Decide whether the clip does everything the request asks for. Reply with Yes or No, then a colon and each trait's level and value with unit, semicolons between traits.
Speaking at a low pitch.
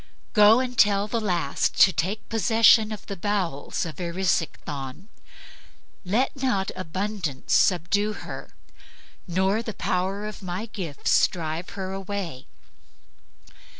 No: high, 195 Hz